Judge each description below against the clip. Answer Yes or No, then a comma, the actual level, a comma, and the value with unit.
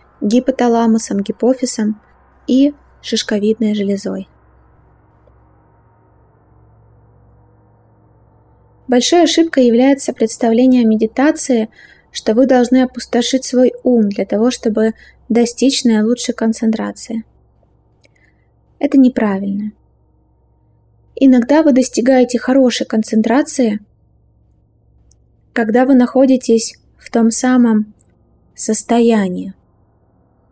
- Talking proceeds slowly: Yes, slow, 75 wpm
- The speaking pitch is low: No, high, 230 Hz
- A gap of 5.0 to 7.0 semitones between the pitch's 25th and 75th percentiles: Yes, wide, 5.6 semitones